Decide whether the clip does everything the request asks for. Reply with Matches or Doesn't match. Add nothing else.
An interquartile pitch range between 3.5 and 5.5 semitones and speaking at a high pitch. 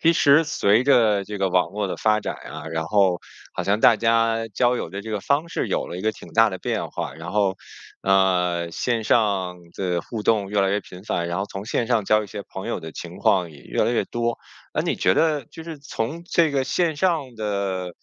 Doesn't match